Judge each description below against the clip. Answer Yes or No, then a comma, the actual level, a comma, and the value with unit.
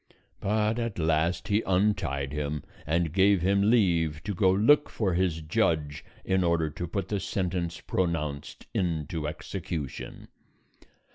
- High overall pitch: No, very low, 85 Hz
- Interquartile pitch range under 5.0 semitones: Yes, average, 4.0 semitones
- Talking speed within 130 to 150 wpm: Yes, slow, 135 wpm